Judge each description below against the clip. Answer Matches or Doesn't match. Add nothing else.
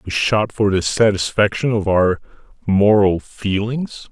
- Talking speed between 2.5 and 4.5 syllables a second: Matches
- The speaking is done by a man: Matches